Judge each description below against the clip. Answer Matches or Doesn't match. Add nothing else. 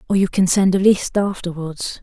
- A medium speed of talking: Doesn't match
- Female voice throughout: Matches